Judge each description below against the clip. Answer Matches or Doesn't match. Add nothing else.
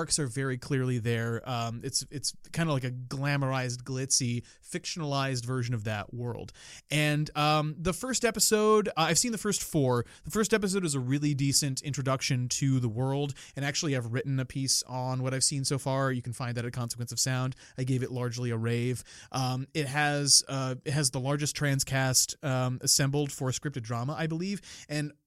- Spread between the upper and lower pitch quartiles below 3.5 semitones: Matches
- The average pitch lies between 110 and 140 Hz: Matches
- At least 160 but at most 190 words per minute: Doesn't match